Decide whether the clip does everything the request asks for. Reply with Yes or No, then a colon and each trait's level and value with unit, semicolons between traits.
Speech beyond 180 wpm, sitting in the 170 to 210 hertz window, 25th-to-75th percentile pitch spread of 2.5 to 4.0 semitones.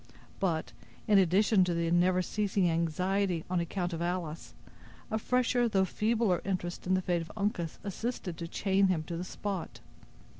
No: average, 165 wpm; medium, 185 Hz; average, 2.8 semitones